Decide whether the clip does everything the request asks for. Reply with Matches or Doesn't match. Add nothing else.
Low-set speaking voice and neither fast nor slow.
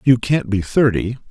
Matches